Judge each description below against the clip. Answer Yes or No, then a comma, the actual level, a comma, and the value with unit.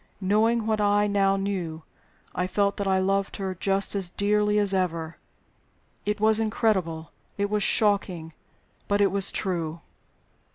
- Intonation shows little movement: Yes, narrow, 2.1 semitones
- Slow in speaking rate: No, average, 150 wpm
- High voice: Yes, high, 200 Hz